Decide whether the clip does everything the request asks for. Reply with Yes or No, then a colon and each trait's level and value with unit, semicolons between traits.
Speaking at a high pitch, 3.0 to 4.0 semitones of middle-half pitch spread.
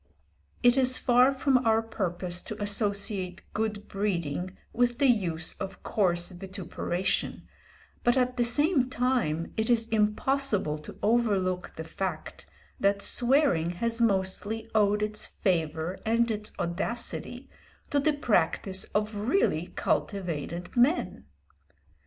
No: high, 210 Hz; average, 4.8 semitones